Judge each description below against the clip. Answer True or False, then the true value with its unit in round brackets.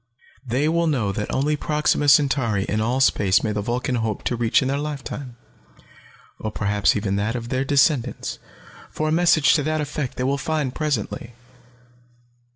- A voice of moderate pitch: False (130 Hz)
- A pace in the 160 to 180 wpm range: True (175 wpm)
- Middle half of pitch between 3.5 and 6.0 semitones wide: True (4.7 semitones)